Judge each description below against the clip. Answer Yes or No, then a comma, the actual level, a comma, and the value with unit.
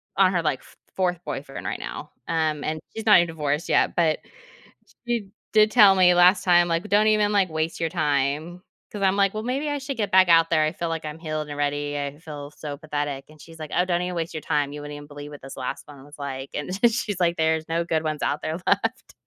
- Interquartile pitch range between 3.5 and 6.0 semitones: Yes, average, 4.1 semitones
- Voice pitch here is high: No, medium, 165 Hz